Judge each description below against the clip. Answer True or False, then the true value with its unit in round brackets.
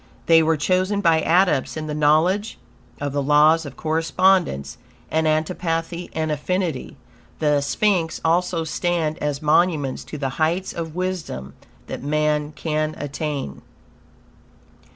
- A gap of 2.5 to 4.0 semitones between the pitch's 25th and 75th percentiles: True (2.8 semitones)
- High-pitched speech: False (160 Hz)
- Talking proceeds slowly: True (130 wpm)